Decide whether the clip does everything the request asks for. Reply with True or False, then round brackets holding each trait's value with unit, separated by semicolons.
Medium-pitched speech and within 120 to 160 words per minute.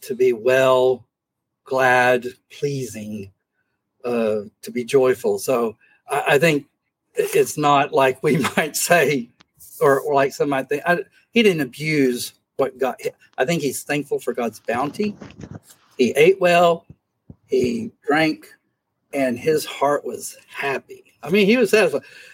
True (145 Hz; 140 wpm)